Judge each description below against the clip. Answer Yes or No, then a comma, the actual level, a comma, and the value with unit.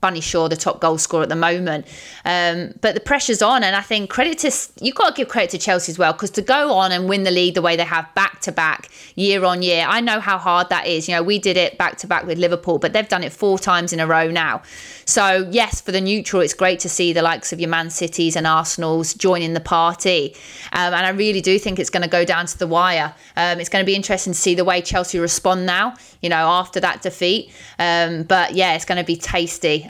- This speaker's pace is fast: Yes, fast, 265 wpm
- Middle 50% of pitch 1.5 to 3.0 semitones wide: Yes, narrow, 2.5 semitones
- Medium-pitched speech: Yes, medium, 180 Hz